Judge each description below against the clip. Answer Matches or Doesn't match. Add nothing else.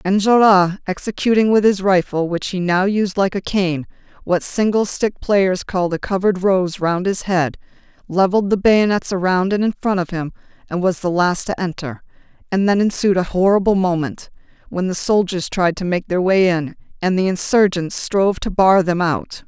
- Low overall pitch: Doesn't match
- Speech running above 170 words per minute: Matches